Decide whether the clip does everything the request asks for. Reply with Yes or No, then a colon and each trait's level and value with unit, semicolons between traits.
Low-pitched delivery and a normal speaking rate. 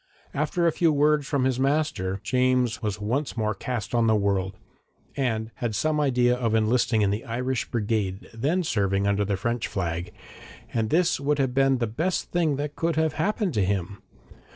Yes: low, 120 Hz; average, 185 wpm